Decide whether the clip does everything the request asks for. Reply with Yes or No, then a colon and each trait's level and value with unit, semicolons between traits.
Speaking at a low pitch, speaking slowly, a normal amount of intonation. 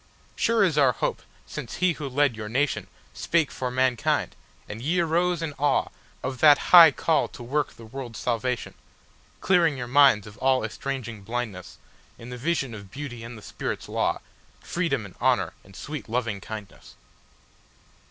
No: low, 130 Hz; average, 145 wpm; average, 4.4 semitones